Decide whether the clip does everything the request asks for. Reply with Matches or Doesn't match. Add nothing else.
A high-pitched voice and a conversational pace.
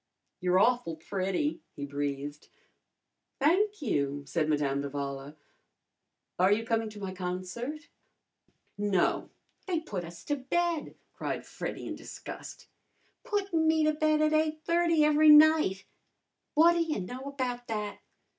Doesn't match